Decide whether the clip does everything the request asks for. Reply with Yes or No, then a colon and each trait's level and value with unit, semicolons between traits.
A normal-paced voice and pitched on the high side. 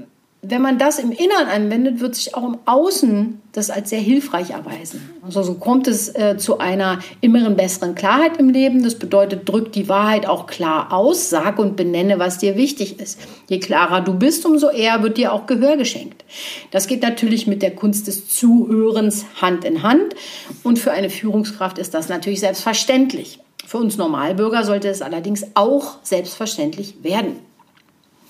Yes: average, 175 wpm; high, 215 Hz